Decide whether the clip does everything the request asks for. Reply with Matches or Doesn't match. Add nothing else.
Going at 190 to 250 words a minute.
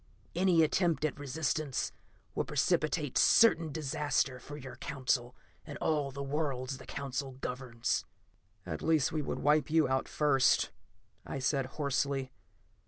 Doesn't match